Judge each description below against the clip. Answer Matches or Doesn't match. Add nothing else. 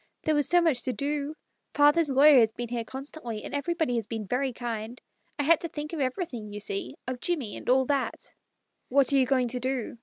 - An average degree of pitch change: Matches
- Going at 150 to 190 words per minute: Doesn't match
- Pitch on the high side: Matches